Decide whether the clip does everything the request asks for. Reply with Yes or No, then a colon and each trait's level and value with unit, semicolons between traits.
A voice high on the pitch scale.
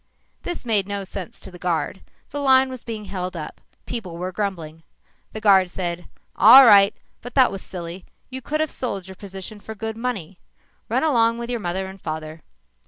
Yes: high, 200 Hz